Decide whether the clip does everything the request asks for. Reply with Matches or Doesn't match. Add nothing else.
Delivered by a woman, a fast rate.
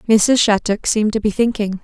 Doesn't match